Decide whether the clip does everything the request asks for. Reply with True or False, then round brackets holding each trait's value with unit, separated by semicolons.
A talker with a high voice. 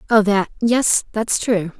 True (215 Hz)